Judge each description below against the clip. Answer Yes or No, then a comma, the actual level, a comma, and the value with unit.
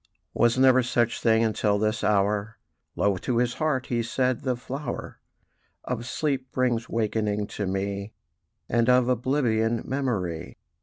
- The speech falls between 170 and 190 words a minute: No, average, 140 wpm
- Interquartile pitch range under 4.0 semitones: Yes, average, 3.2 semitones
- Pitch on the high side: No, low, 115 Hz